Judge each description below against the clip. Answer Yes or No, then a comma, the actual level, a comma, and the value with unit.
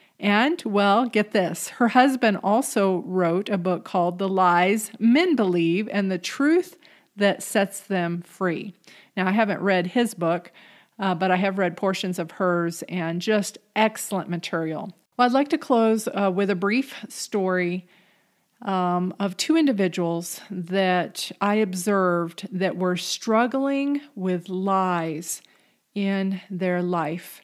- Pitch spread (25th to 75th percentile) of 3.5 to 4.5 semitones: No, average, 3.0 semitones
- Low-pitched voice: No, high, 195 Hz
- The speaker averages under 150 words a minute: Yes, average, 140 wpm